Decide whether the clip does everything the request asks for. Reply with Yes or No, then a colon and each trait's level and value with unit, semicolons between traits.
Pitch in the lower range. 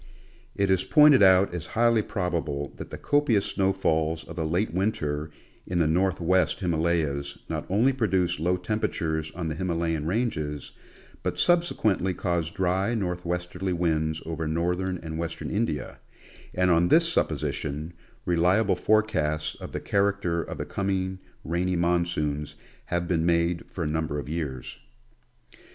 Yes: very low, 85 Hz